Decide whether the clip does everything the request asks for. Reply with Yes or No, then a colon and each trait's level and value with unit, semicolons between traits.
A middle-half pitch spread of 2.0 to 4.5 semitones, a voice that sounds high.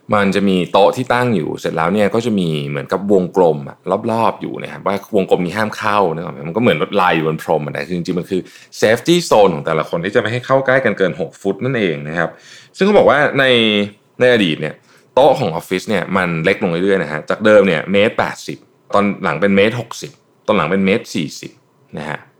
No: average, 3.9 semitones; low, 100 Hz